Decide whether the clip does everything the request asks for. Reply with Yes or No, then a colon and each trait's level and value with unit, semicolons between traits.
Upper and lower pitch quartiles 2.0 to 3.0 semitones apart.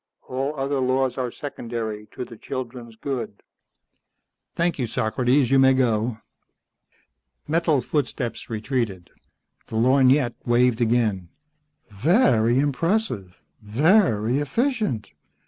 No: average, 3.8 semitones